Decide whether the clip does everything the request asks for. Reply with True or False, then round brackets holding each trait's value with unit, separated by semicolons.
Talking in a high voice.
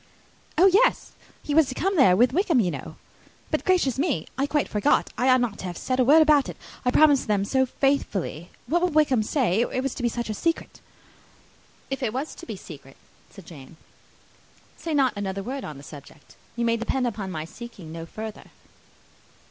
True (245 Hz)